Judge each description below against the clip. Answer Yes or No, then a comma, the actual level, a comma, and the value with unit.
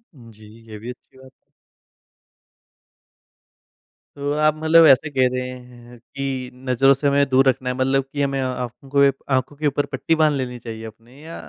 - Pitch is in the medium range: No, low, 130 Hz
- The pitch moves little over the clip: Yes, narrow, 2.2 semitones